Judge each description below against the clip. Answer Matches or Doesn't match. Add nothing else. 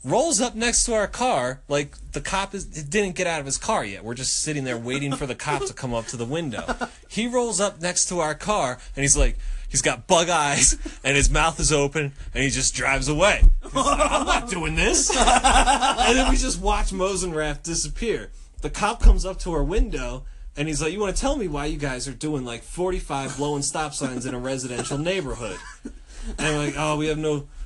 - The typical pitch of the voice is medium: Matches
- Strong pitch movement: Matches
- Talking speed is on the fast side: Matches